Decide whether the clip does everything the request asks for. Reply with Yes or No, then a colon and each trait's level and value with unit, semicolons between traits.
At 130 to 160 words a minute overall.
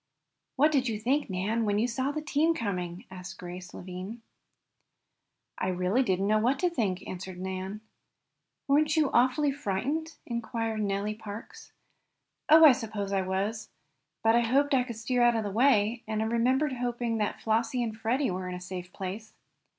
No: average, 180 wpm